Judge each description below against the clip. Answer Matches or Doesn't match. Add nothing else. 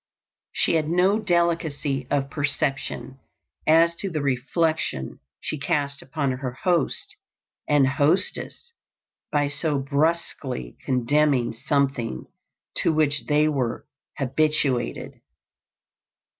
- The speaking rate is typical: Doesn't match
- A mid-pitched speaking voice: Matches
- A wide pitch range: Doesn't match